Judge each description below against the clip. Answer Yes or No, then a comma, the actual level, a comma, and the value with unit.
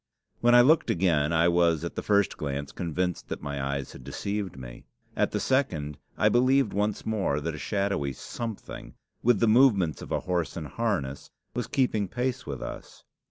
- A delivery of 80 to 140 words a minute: No, average, 185 wpm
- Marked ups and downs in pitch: Yes, wide, 7.3 semitones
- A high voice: No, very low, 90 Hz